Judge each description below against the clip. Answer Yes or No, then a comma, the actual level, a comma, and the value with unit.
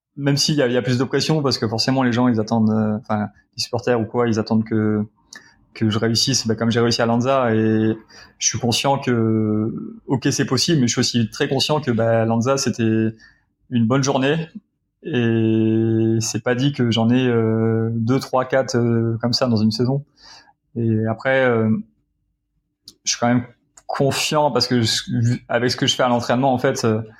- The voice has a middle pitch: No, low, 120 Hz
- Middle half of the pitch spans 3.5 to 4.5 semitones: No, average, 3.0 semitones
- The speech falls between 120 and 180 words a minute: No, average, 200 wpm